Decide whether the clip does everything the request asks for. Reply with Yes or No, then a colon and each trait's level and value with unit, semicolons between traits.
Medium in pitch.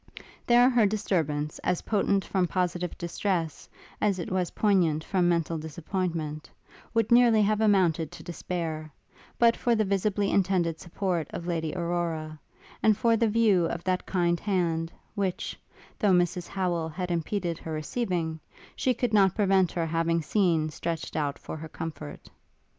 Yes: medium, 175 Hz